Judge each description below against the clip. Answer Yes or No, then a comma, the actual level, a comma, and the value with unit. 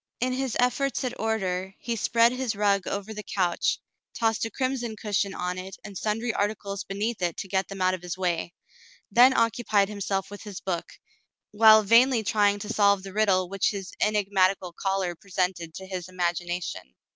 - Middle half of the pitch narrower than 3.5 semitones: Yes, average, 2.9 semitones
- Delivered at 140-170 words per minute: No, average, 180 wpm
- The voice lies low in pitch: No, high, 200 Hz